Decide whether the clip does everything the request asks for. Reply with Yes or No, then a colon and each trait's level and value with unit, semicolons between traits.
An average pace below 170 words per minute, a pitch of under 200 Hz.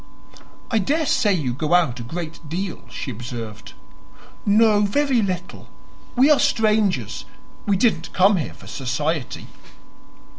Yes: slow, 135 wpm; medium, 185 Hz